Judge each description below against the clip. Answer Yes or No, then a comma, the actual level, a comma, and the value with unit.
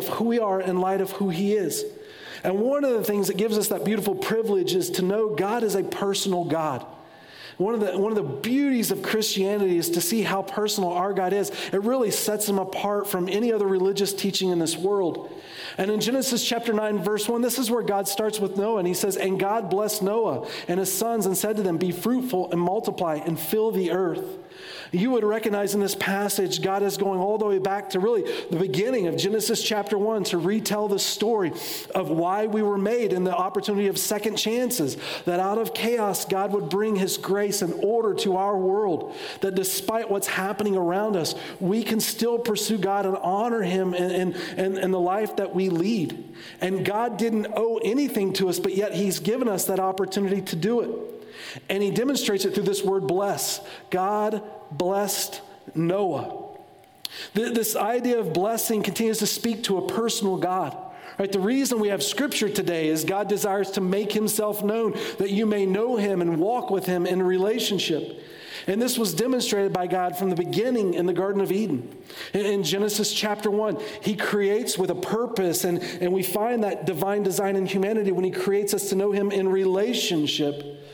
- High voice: Yes, high, 200 Hz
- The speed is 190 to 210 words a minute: Yes, average, 200 wpm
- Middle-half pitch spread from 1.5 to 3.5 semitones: Yes, narrow, 2.4 semitones